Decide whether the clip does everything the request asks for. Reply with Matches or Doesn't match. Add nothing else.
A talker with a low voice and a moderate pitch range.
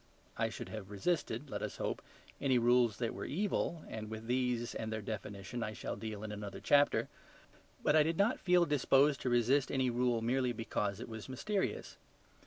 Matches